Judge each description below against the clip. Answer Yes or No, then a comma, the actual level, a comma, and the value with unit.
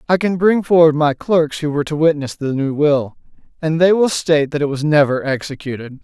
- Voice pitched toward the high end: No, medium, 150 Hz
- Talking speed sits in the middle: No, fast, 220 wpm